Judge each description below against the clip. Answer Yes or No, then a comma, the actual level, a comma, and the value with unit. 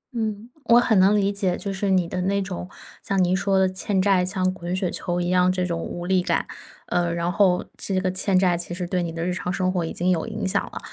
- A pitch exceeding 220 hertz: No, medium, 185 Hz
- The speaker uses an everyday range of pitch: No, narrow, 1.6 semitones